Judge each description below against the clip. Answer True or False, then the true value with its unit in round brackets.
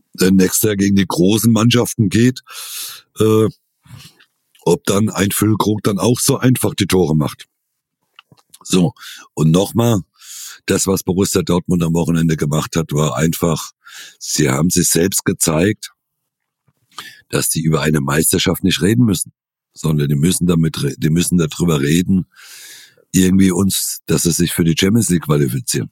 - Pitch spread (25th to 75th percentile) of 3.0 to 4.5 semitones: True (4.2 semitones)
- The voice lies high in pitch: False (95 Hz)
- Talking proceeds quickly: False (145 wpm)